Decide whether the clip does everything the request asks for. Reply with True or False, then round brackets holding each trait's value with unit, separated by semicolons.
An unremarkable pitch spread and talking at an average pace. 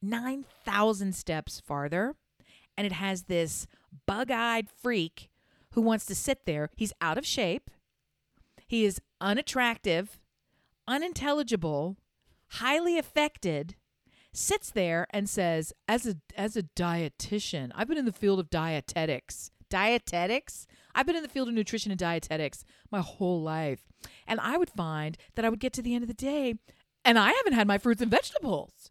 False (6.2 semitones; 155 wpm)